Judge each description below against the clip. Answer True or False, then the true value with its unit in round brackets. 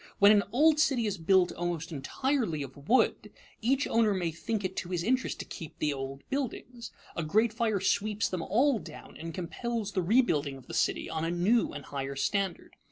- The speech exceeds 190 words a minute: True (200 wpm)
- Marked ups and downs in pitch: True (6.2 semitones)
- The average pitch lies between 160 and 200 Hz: True (190 Hz)